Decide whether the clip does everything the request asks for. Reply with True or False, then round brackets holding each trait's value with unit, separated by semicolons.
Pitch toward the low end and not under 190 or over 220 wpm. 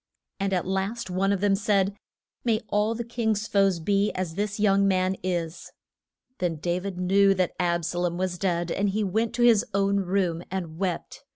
False (195 Hz; 195 wpm)